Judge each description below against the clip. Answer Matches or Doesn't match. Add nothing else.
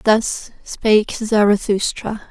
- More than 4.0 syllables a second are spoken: Doesn't match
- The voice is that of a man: Doesn't match